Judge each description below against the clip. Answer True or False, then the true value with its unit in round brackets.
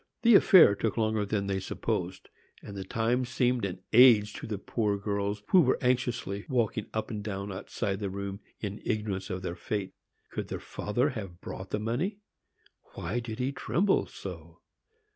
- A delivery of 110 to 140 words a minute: False (175 wpm)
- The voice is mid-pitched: False (105 Hz)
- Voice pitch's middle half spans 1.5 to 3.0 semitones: False (3.5 semitones)